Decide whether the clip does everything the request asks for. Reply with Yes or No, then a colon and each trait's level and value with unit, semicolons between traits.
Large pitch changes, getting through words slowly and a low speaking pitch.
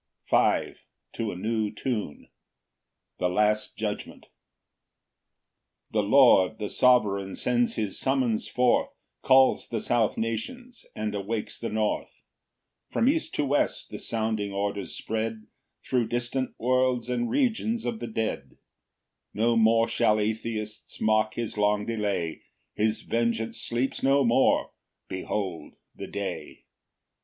No: average, 2.7 semitones; slow, 130 wpm; low, 110 Hz